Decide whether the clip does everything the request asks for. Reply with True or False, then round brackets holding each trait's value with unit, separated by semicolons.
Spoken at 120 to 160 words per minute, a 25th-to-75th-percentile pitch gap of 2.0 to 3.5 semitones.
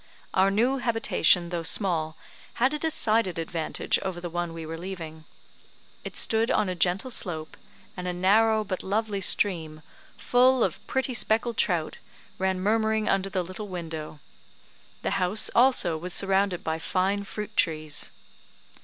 False (150 wpm; 4.4 semitones)